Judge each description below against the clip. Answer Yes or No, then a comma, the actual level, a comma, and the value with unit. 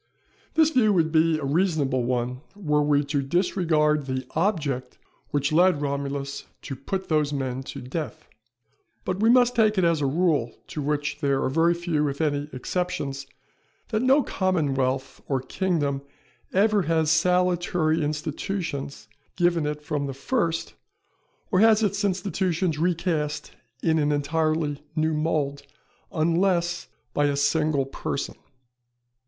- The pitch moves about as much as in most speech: Yes, average, 4.0 semitones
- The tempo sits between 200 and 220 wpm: No, average, 140 wpm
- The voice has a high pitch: No, medium, 155 Hz